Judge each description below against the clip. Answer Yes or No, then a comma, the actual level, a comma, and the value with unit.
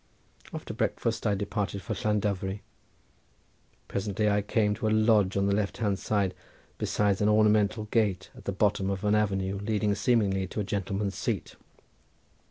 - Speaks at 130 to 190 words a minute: Yes, average, 155 wpm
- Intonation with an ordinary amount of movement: No, narrow, 1.5 semitones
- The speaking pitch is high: No, low, 105 Hz